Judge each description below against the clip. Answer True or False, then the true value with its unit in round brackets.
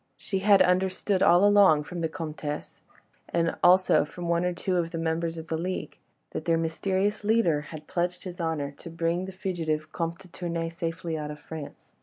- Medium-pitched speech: True (170 Hz)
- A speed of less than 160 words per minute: False (195 wpm)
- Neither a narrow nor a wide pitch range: False (2.3 semitones)